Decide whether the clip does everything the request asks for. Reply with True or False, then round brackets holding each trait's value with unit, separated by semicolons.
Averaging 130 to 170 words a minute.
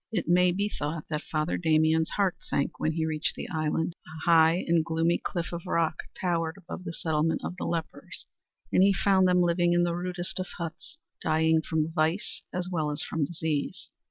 False (195 wpm)